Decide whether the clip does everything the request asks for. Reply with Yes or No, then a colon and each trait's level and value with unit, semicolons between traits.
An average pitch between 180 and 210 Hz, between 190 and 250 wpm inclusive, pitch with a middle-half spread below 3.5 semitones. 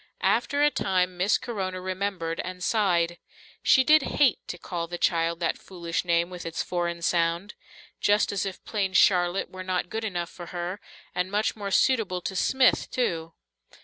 No: medium, 185 Hz; average, 175 wpm; average, 2.8 semitones